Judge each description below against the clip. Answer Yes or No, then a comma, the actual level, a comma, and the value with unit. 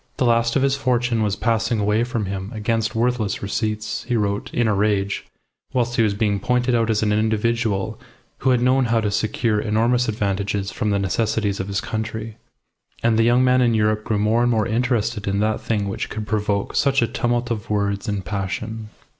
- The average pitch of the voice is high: No, low, 110 Hz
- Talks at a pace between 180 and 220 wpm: Yes, fast, 205 wpm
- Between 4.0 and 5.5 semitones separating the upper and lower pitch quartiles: No, narrow, 2.4 semitones